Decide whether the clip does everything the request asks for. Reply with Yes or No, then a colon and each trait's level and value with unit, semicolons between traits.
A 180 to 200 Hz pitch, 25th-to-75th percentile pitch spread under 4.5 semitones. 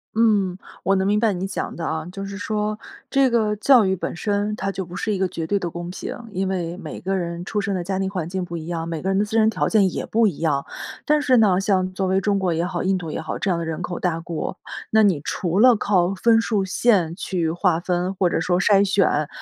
Yes: high, 190 Hz; average, 2.9 semitones